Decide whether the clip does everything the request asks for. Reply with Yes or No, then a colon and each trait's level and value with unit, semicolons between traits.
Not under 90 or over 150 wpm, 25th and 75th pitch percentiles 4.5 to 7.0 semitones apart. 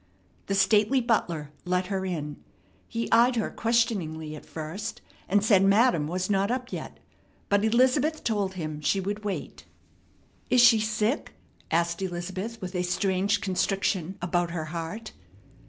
No: average, 145 wpm; average, 4.1 semitones